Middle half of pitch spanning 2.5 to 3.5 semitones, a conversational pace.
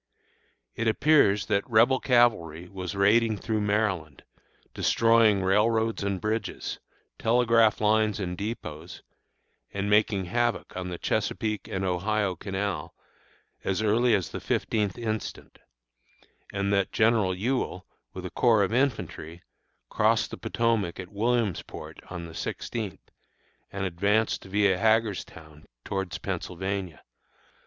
No: average, 3.2 semitones; slow, 120 wpm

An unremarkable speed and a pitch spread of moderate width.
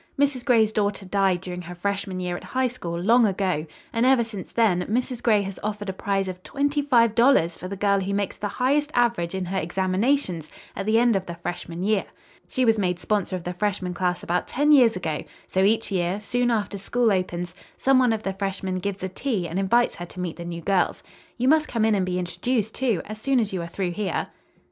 No: fast, 230 wpm; average, 4.3 semitones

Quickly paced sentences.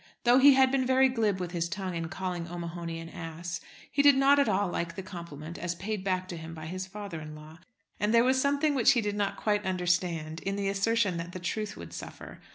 Yes: fast, 240 wpm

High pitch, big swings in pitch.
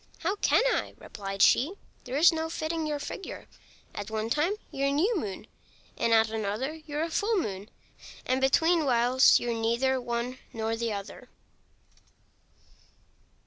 Yes: very high, 260 Hz; wide, 6.0 semitones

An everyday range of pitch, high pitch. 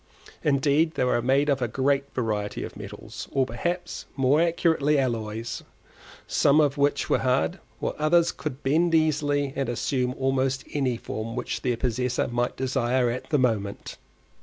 No: average, 3.1 semitones; low, 135 Hz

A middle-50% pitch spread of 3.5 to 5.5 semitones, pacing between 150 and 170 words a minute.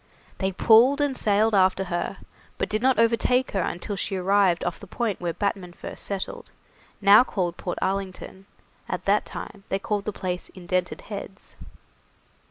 No: average, 2.7 semitones; average, 165 wpm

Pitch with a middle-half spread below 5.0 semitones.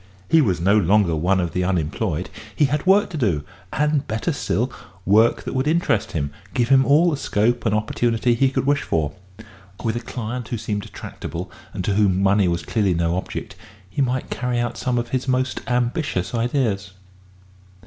No: average, 5.3 semitones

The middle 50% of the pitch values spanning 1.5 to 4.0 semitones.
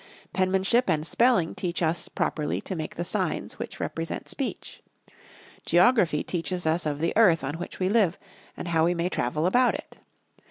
Yes: average, 2.8 semitones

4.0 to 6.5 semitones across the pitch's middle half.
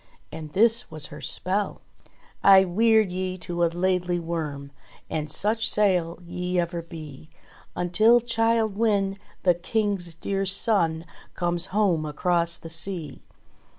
No: average, 3.4 semitones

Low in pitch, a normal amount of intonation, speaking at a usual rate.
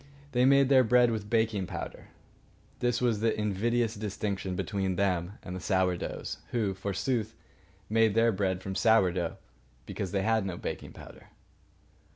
Yes: low, 105 Hz; average, 3.3 semitones; average, 160 wpm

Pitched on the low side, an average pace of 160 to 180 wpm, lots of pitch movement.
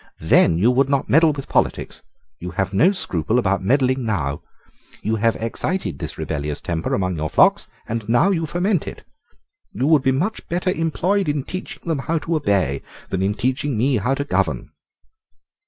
Yes: low, 130 Hz; average, 175 wpm; wide, 8.2 semitones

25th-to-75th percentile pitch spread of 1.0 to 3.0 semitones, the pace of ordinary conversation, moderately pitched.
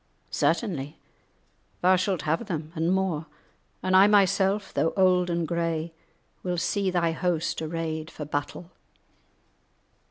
No: average, 2.7 semitones; slow, 125 wpm; medium, 170 Hz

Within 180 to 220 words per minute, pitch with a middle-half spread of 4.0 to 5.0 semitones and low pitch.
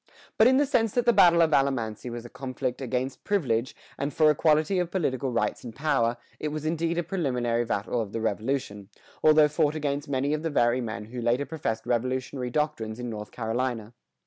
Yes: average, 200 wpm; average, 4.7 semitones; low, 130 Hz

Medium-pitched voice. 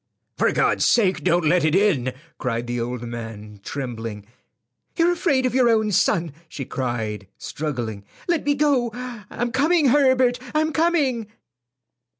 Yes: medium, 180 Hz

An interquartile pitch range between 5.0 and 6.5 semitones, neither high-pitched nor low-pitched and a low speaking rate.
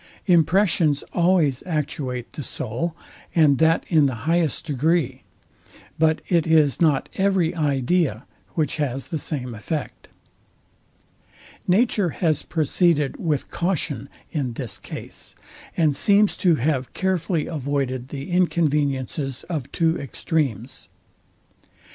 No: average, 3.9 semitones; medium, 155 Hz; slow, 110 wpm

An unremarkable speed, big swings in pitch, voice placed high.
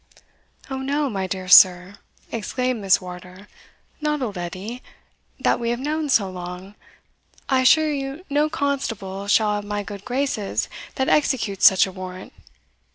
Yes: average, 150 wpm; wide, 6.1 semitones; high, 210 Hz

